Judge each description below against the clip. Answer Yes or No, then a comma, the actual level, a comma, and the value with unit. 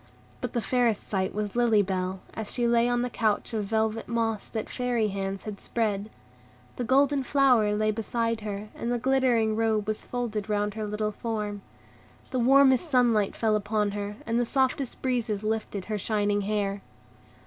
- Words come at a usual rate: Yes, average, 175 wpm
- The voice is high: Yes, high, 220 Hz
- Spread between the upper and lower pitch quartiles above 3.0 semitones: No, narrow, 2.5 semitones